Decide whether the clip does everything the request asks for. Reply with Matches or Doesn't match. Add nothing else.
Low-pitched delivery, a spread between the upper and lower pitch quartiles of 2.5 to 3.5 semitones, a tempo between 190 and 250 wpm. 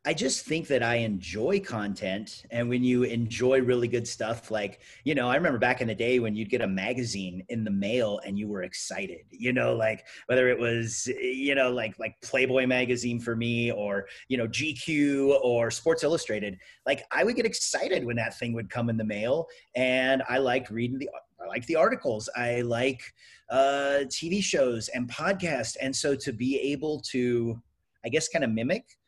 Matches